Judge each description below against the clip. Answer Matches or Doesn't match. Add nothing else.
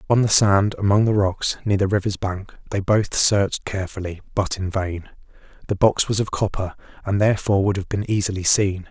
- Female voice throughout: Doesn't match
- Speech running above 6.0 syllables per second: Doesn't match